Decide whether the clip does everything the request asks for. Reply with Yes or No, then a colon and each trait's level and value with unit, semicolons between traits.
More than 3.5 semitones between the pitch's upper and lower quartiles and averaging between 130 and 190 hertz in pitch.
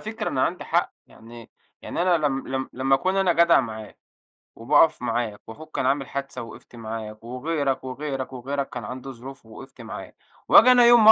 Yes: average, 4.5 semitones; low, 135 Hz